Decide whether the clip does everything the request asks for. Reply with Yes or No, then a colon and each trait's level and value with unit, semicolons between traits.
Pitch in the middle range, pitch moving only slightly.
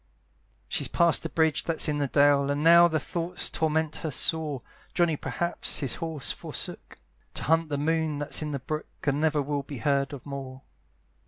Yes: medium, 150 Hz; narrow, 2.3 semitones